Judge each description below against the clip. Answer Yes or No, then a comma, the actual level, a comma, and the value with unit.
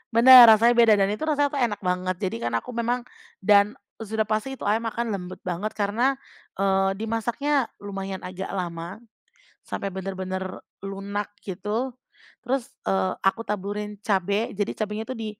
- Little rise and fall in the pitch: No, average, 3.0 semitones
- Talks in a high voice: Yes, high, 205 Hz